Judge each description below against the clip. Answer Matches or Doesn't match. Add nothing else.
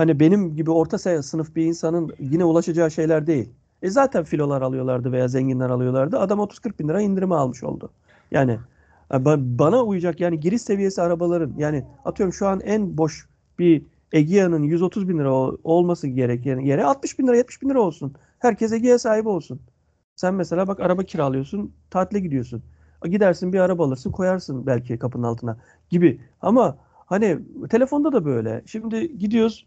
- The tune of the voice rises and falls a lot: Matches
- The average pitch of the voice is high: Doesn't match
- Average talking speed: Doesn't match